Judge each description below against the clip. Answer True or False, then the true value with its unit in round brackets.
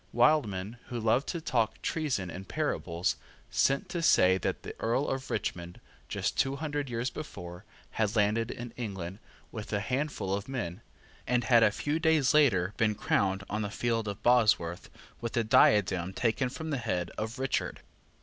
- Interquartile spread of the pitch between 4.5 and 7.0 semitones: True (5.1 semitones)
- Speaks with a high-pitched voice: False (115 Hz)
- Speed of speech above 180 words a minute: False (170 wpm)